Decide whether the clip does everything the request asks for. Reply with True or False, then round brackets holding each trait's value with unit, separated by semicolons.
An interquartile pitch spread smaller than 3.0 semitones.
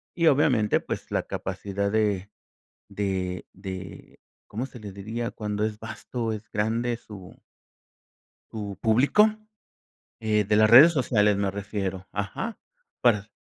True (2.6 semitones)